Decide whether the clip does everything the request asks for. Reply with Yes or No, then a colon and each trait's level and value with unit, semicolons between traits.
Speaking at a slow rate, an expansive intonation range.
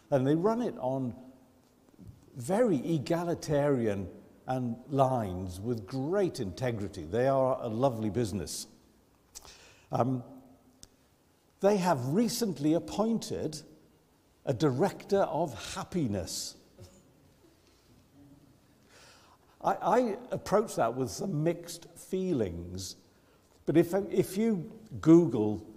Yes: slow, 90 wpm; wide, 6.7 semitones